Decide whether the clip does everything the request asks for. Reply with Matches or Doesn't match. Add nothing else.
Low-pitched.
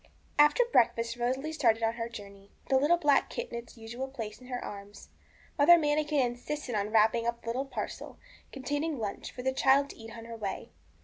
Doesn't match